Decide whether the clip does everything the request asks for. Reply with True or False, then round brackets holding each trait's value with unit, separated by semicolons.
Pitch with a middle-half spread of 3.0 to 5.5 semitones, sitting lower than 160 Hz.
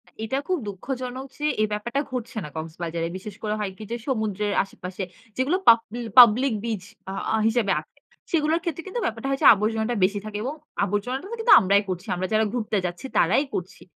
False (4.6 semitones; 220 Hz)